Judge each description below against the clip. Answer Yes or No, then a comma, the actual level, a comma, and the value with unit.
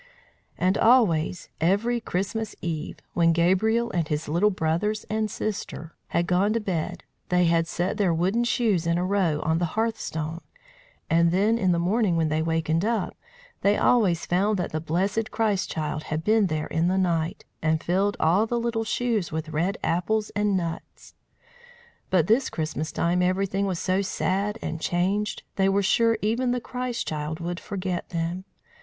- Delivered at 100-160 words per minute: No, average, 175 wpm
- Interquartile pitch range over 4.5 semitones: No, average, 4.1 semitones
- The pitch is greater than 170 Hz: Yes, medium, 185 Hz